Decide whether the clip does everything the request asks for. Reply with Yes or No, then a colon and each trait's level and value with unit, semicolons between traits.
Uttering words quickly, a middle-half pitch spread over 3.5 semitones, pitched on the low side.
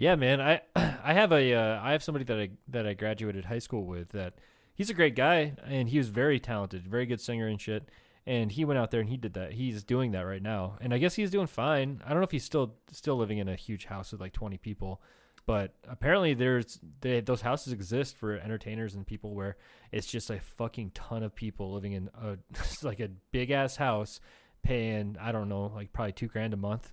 Yes: fast, 235 wpm; average, 4.2 semitones; low, 115 Hz